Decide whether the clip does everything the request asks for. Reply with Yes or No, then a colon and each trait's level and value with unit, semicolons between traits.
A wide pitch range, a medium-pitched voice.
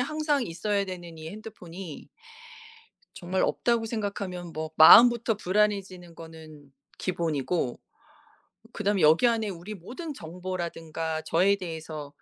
No: average, 4.4 semitones; medium, 180 Hz